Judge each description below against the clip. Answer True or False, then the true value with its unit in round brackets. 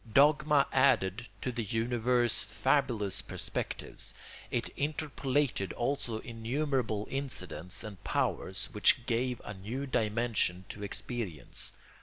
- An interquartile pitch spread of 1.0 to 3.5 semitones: False (4.5 semitones)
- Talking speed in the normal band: False (105 wpm)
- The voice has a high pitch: False (120 Hz)